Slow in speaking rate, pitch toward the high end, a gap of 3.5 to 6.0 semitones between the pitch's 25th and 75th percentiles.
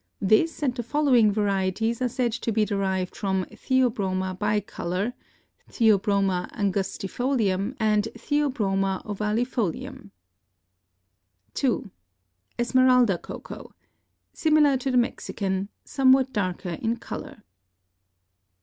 Yes: slow, 90 wpm; high, 215 Hz; average, 4.4 semitones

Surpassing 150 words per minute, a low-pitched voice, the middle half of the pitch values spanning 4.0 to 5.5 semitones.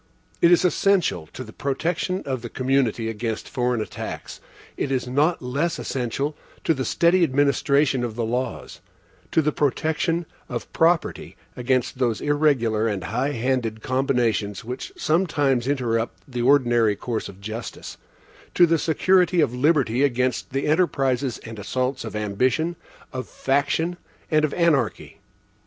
No: average, 145 wpm; low, 130 Hz; average, 4.4 semitones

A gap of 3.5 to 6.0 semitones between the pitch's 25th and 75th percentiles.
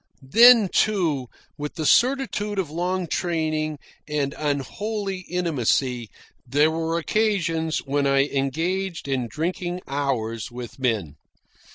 Yes: average, 5.0 semitones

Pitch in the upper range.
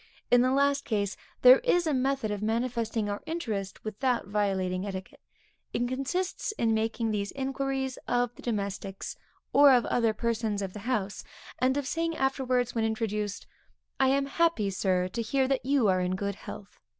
Yes: high, 235 Hz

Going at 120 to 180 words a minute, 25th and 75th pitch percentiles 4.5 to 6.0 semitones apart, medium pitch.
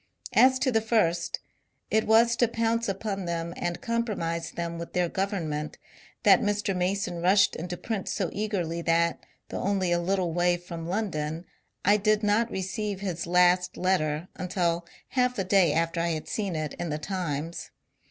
No: average, 170 wpm; average, 3.5 semitones; medium, 180 Hz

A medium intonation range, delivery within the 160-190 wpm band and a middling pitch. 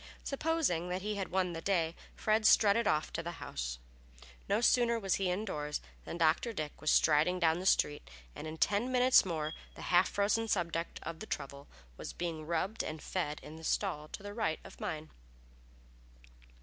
Yes: average, 4.7 semitones; average, 180 wpm; medium, 175 Hz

